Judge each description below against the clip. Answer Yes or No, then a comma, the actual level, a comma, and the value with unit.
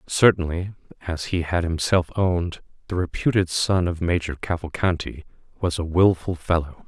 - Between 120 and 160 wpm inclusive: Yes, average, 140 wpm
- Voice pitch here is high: No, very low, 85 Hz